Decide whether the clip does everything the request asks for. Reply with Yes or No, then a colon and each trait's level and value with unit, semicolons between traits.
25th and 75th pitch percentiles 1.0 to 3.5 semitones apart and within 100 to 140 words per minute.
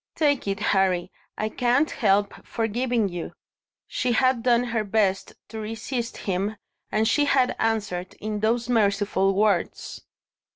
Yes: average, 3.2 semitones; slow, 135 wpm